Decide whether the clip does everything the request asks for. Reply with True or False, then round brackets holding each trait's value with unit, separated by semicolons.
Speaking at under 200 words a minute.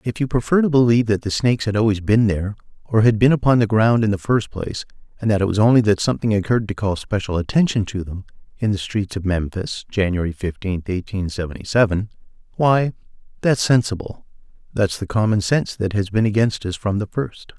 False (205 wpm)